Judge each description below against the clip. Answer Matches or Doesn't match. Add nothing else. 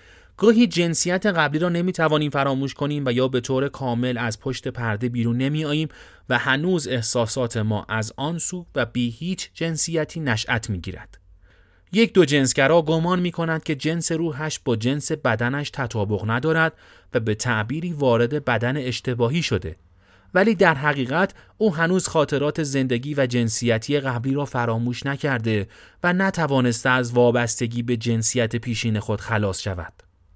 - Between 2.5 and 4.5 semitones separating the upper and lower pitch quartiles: Doesn't match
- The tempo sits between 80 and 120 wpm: Doesn't match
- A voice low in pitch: Matches